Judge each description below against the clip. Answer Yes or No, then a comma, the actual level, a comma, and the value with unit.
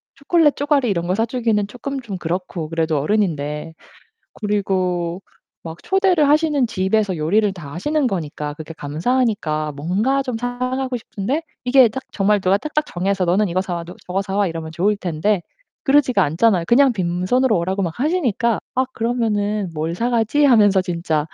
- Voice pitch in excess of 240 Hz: No, high, 205 Hz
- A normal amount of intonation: No, wide, 6.3 semitones